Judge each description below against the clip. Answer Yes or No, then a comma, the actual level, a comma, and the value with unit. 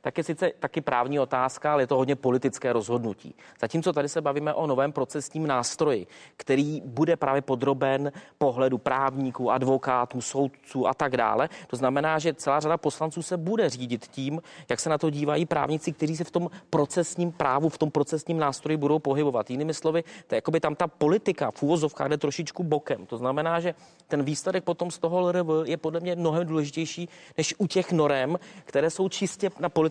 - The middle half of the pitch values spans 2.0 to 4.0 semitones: Yes, average, 3.6 semitones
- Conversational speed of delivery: No, fast, 185 wpm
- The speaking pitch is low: No, medium, 155 Hz